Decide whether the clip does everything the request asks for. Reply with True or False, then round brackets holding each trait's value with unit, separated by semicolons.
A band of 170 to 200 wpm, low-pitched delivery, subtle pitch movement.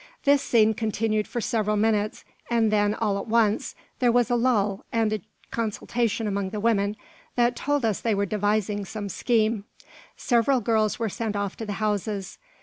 False (175 wpm; 215 Hz; 2.1 semitones)